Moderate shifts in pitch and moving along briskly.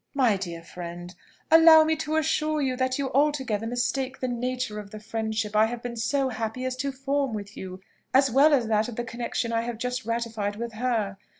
Yes: average, 3.6 semitones; fast, 210 wpm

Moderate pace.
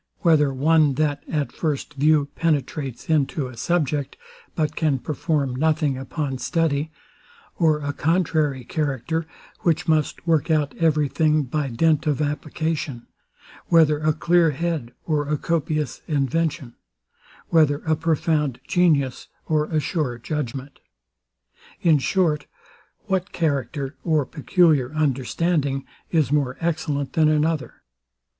No: slow, 125 wpm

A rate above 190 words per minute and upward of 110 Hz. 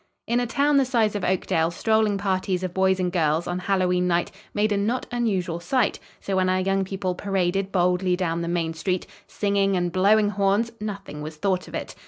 Yes: fast, 205 wpm; high, 190 Hz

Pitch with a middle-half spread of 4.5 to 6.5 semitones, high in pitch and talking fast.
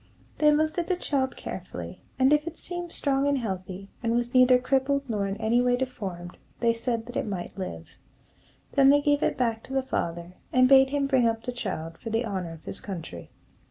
Yes: wide, 5.6 semitones; high, 245 Hz; fast, 215 wpm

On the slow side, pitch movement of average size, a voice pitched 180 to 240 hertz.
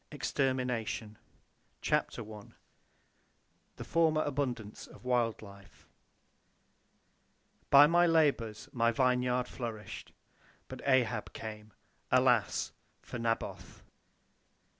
No: slow, 85 wpm; average, 3.6 semitones; low, 120 Hz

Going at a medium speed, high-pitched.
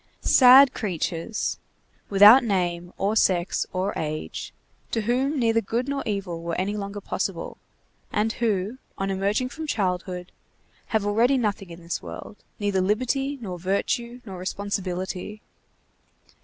No: slow, 130 wpm; high, 205 Hz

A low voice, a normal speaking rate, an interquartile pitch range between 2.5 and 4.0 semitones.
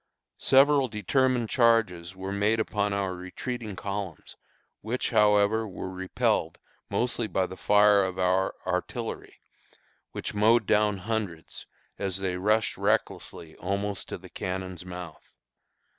No: low, 100 Hz; slow, 125 wpm; average, 3.0 semitones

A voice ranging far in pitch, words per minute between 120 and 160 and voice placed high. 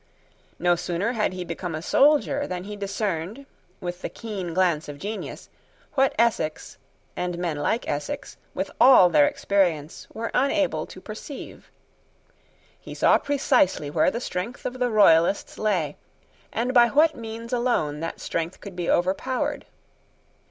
Yes: wide, 5.9 semitones; average, 145 wpm; high, 195 Hz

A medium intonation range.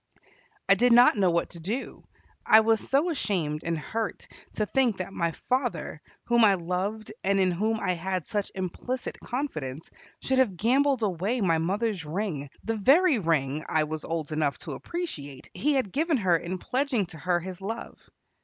No: wide, 6.2 semitones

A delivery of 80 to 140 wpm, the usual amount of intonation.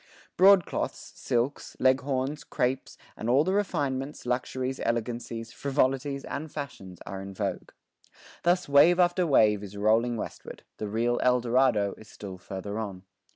Yes: slow, 135 wpm; average, 4.6 semitones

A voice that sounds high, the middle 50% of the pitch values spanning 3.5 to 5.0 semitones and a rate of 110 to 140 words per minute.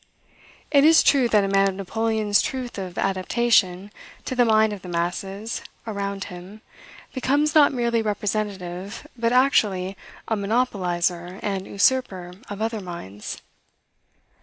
Yes: high, 205 Hz; average, 3.8 semitones; slow, 135 wpm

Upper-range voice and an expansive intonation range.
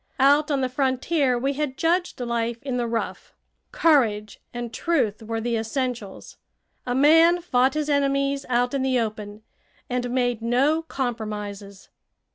No: very high, 250 Hz; average, 3.5 semitones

